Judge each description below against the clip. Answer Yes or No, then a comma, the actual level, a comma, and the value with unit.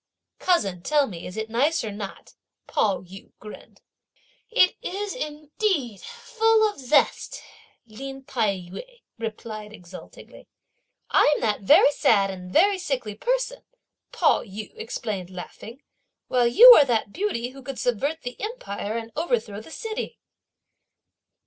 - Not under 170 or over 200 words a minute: No, slow, 135 wpm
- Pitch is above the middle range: Yes, high, 245 Hz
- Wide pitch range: Yes, wide, 7.6 semitones